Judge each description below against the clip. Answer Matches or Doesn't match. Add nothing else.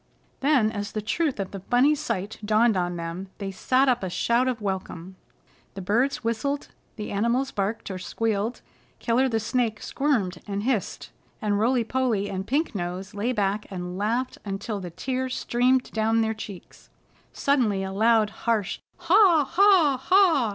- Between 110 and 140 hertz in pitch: Doesn't match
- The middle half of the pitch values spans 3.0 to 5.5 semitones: Matches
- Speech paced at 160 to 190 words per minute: Matches